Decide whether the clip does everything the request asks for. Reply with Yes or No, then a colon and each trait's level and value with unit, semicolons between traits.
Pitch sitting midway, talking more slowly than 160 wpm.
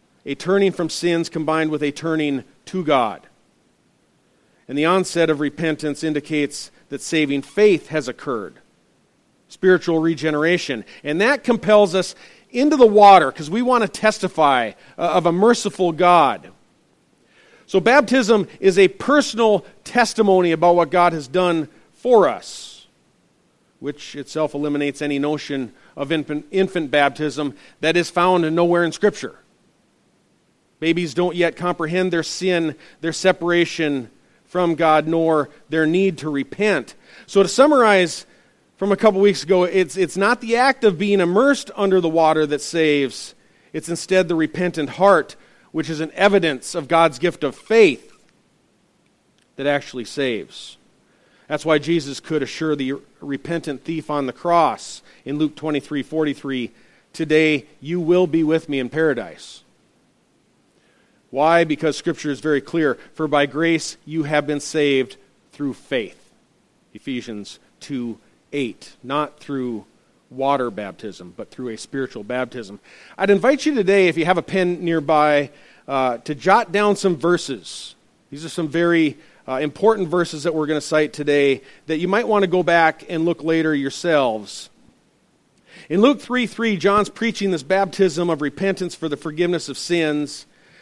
Yes: medium, 165 Hz; average, 150 wpm